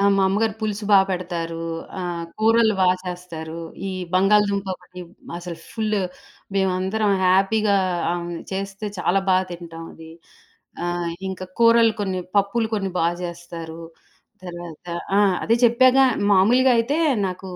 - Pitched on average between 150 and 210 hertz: Yes, high, 190 Hz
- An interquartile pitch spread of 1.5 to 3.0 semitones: No, average, 3.6 semitones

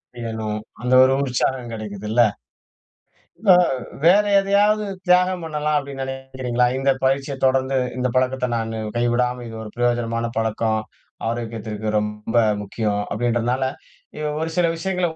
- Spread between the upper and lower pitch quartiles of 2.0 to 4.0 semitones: Yes, average, 3.5 semitones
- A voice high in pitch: No, low, 125 Hz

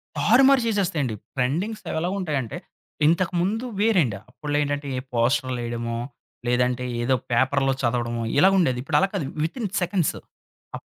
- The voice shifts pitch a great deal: Yes, wide, 7.0 semitones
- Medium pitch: Yes, medium, 145 Hz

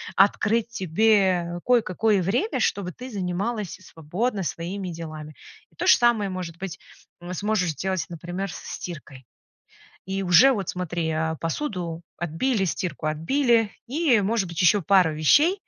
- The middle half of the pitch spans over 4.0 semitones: Yes, average, 4.4 semitones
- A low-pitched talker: No, medium, 185 Hz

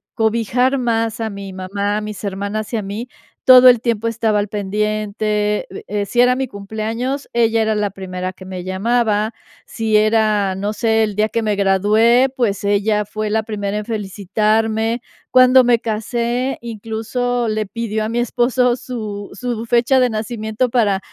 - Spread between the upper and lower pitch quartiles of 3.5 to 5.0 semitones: No, narrow, 2.4 semitones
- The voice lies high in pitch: Yes, high, 220 Hz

